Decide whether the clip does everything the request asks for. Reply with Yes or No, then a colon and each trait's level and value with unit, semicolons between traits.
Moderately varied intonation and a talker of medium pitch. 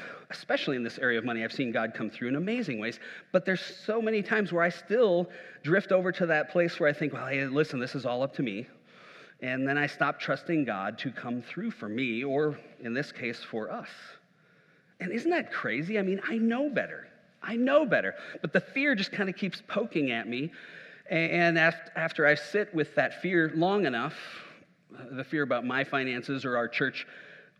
No: wide, 5.7 semitones; medium, 170 Hz